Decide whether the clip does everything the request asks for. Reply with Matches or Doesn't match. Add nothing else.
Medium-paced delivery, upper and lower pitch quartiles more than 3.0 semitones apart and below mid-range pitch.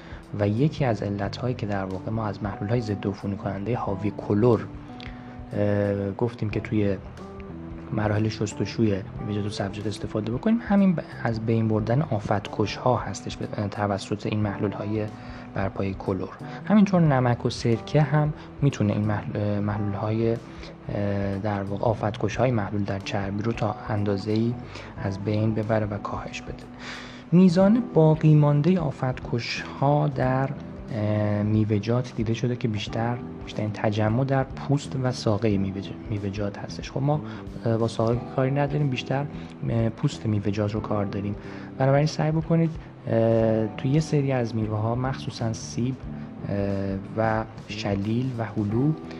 Matches